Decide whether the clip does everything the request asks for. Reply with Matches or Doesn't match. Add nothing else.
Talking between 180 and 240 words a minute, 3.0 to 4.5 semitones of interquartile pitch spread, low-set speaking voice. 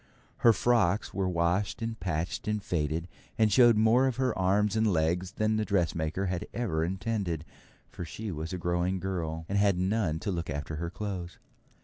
Matches